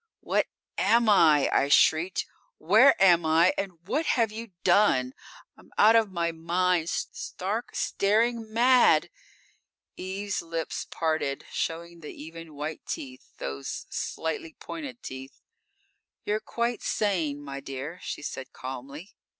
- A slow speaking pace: Yes, slow, 125 wpm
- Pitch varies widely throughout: Yes, wide, 5.7 semitones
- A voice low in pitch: No, medium, 170 Hz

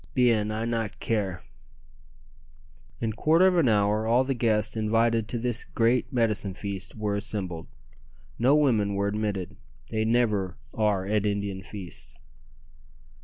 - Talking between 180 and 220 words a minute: No, slow, 135 wpm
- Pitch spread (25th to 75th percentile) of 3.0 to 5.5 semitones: No, narrow, 2.5 semitones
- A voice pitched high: No, low, 110 Hz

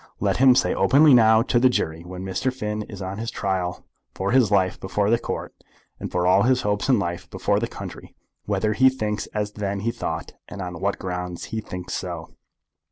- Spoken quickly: Yes, fast, 210 wpm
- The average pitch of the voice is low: Yes, low, 100 Hz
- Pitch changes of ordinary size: Yes, average, 4.0 semitones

